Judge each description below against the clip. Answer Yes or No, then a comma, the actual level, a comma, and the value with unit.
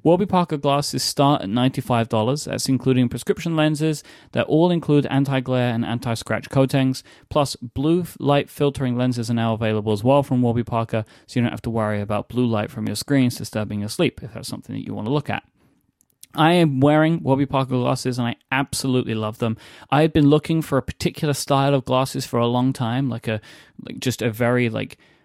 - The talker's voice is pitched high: No, low, 130 Hz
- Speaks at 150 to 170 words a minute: No, average, 200 wpm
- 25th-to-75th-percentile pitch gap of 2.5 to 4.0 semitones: Yes, average, 3.3 semitones